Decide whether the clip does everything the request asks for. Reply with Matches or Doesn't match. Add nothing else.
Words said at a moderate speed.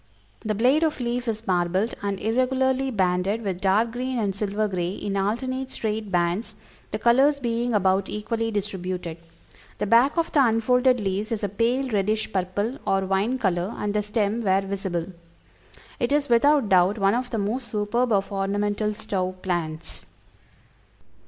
Matches